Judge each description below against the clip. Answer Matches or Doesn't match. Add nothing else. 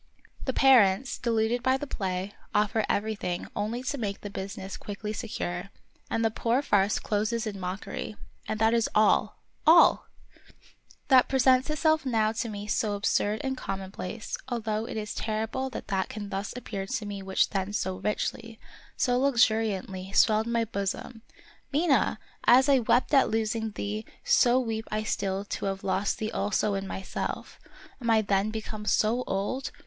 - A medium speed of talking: Matches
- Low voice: Doesn't match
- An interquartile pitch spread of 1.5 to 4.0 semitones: Matches